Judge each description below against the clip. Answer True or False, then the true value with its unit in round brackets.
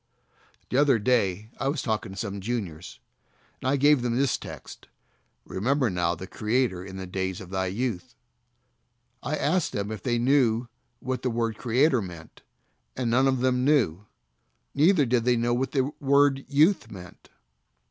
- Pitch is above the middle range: False (120 Hz)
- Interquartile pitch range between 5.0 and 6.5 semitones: True (5.5 semitones)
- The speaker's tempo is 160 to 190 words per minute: True (170 wpm)